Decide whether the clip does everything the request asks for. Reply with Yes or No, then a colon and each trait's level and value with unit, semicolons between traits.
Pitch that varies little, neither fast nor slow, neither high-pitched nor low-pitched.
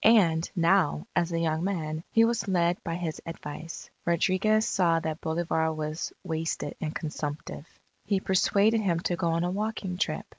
No: average, 3.0 semitones; average, 170 wpm; medium, 170 Hz